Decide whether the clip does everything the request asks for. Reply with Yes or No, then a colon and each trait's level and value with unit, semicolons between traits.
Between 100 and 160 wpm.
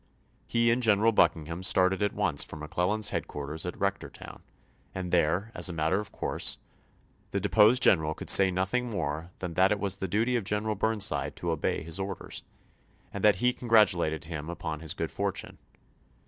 No: average, 175 wpm